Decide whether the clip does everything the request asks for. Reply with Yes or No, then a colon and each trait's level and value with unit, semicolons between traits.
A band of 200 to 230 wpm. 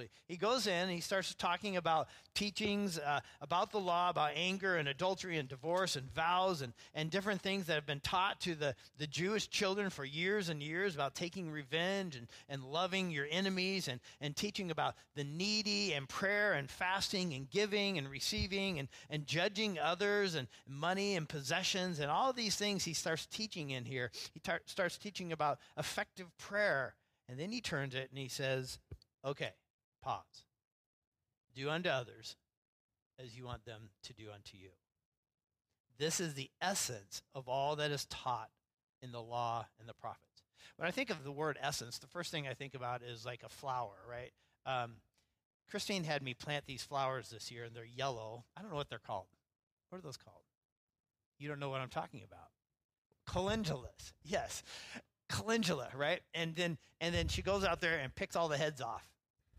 No: average, 185 wpm